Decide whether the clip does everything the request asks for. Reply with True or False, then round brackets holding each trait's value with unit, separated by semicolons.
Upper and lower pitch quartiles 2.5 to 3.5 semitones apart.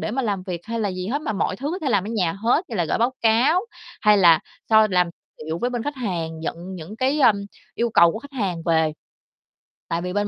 False (5.3 semitones)